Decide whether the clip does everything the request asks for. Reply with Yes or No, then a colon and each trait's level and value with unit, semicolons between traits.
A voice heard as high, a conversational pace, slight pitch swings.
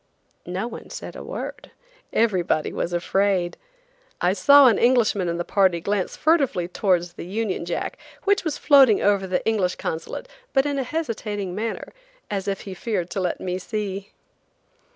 No: high, 200 Hz; average, 165 wpm; average, 4.2 semitones